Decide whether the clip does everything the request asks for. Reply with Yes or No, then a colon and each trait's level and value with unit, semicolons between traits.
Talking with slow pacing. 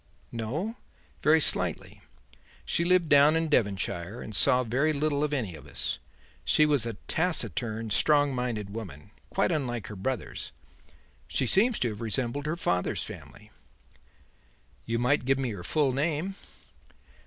No: average, 145 wpm